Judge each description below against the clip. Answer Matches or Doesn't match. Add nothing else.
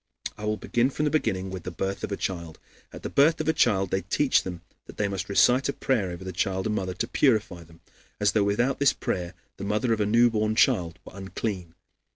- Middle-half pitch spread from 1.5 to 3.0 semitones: Doesn't match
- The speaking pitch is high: Doesn't match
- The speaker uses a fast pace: Matches